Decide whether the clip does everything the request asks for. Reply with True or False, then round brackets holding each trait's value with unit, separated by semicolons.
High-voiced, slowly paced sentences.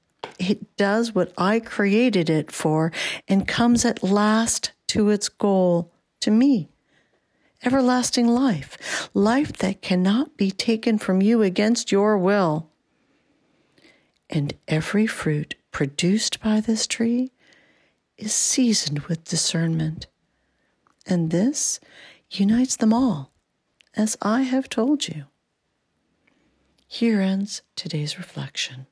True (205 Hz; 110 wpm)